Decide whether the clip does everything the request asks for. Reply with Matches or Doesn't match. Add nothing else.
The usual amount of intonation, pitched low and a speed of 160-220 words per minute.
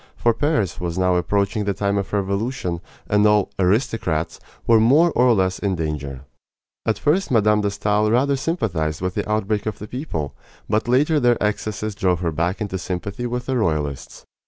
Matches